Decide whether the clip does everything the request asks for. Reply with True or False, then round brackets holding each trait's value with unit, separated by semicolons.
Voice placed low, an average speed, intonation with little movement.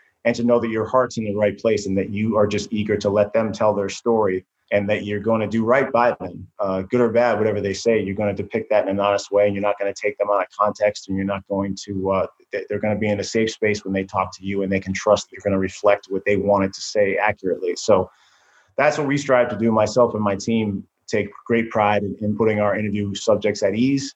False (105 Hz; 265 wpm; 2.2 semitones)